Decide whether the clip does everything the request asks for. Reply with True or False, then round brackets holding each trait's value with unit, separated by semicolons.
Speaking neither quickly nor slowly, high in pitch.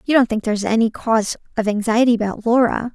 False (225 wpm; 225 Hz)